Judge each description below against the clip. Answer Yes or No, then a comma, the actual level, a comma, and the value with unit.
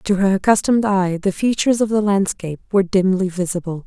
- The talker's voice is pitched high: Yes, high, 195 Hz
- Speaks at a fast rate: No, average, 185 wpm